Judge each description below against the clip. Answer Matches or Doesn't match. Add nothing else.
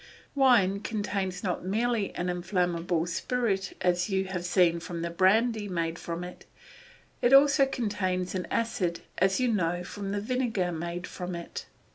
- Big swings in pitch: Doesn't match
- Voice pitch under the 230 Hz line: Matches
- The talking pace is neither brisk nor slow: Matches